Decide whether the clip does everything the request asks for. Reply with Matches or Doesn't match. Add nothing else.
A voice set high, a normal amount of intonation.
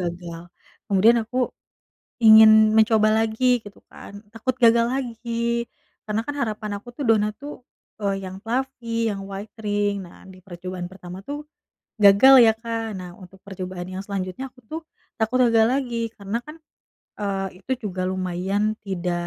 Matches